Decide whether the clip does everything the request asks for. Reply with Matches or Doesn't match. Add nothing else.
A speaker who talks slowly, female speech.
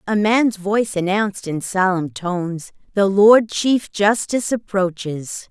Matches